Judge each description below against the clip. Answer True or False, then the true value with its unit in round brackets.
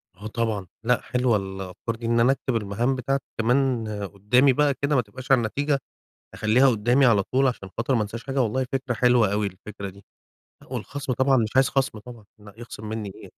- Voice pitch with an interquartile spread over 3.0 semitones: True (3.8 semitones)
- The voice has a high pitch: False (120 Hz)